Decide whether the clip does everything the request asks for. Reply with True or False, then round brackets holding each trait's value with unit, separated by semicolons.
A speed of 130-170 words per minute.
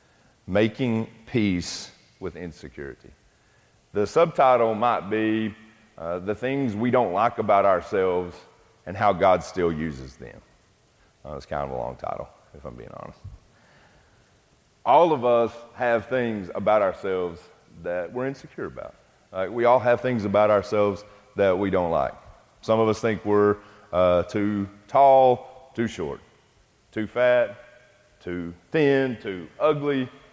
True (140 wpm)